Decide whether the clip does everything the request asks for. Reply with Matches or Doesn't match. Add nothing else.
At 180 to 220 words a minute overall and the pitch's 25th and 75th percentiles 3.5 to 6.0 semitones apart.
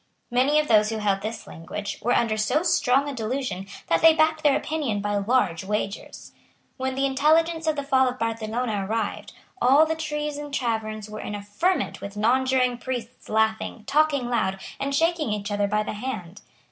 Matches